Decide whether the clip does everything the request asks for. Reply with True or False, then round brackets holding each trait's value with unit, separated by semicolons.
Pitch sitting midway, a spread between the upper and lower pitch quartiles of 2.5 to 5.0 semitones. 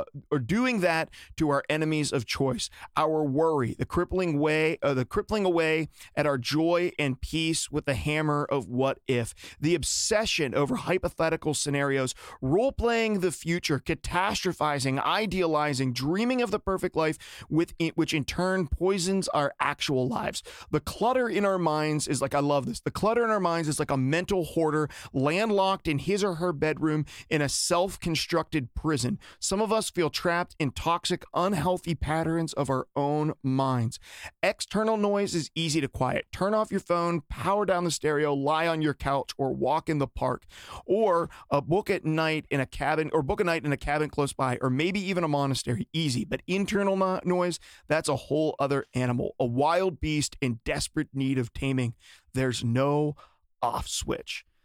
True (155 Hz; 4.1 semitones)